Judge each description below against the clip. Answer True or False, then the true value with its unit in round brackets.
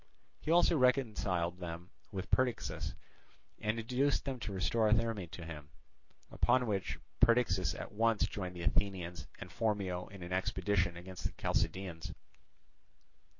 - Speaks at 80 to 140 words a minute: True (135 wpm)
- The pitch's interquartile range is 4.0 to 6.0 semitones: True (4.4 semitones)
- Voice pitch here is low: True (95 Hz)